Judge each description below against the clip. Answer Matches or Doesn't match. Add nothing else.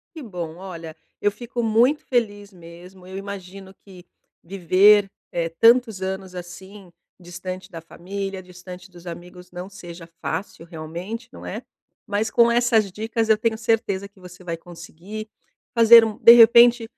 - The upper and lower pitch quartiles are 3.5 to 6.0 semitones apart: Matches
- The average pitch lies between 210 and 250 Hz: Doesn't match